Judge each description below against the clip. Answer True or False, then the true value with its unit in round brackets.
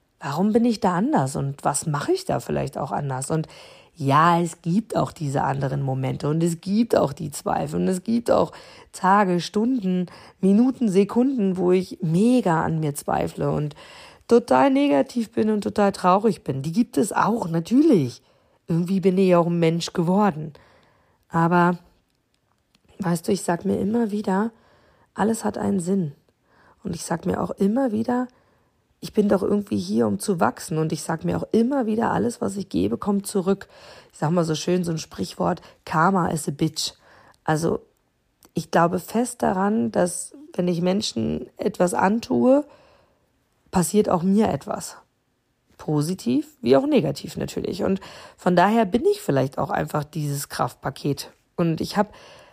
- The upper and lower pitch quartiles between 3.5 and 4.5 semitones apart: False (4.9 semitones)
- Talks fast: False (165 wpm)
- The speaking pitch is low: False (190 Hz)